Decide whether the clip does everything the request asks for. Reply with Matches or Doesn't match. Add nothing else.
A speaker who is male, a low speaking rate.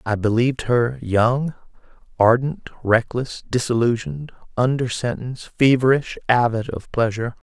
Matches